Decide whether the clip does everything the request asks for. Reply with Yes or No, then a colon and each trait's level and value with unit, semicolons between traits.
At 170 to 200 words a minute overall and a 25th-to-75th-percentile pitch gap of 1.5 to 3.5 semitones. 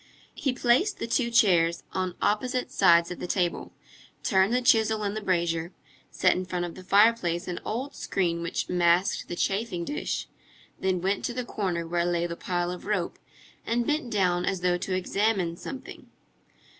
No: average, 180 wpm; average, 4.2 semitones